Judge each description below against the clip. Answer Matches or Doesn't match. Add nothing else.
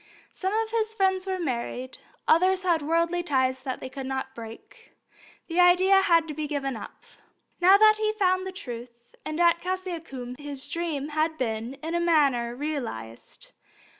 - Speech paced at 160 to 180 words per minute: Matches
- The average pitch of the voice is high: Matches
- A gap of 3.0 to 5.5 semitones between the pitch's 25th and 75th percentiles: Doesn't match